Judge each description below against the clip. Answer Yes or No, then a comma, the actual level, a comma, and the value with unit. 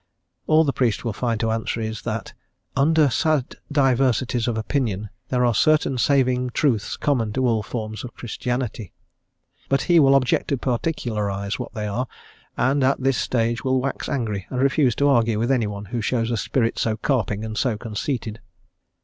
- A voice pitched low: Yes, low, 120 Hz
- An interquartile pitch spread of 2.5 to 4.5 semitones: Yes, average, 3.4 semitones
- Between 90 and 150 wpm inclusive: No, average, 175 wpm